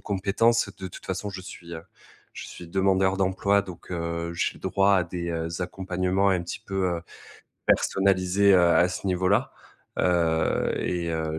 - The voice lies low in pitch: Yes, very low, 95 Hz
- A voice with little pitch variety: Yes, narrow, 2.2 semitones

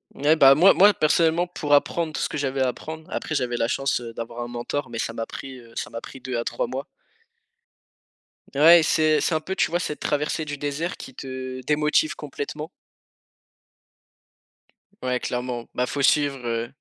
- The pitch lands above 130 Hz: Yes, medium, 140 Hz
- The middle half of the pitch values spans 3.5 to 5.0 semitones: Yes, average, 3.8 semitones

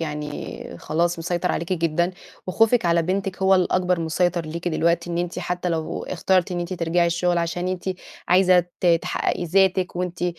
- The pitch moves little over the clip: Yes, narrow, 1.4 semitones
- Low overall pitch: No, medium, 175 Hz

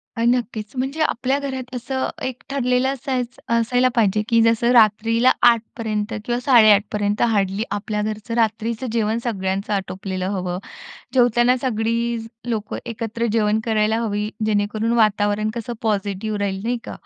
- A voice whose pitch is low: No, high, 225 Hz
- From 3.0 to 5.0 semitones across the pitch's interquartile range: No, narrow, 2.4 semitones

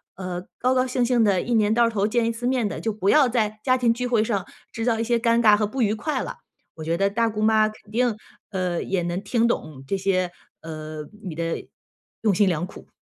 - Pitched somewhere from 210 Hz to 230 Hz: Yes, high, 215 Hz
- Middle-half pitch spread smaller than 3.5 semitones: No, average, 3.8 semitones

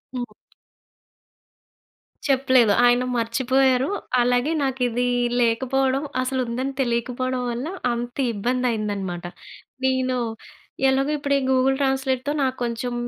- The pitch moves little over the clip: Yes, narrow, 1.7 semitones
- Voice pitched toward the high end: Yes, very high, 255 Hz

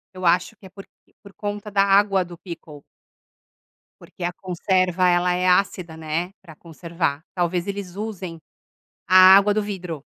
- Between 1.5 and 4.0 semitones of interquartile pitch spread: Yes, narrow, 2.4 semitones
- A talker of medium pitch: Yes, medium, 180 Hz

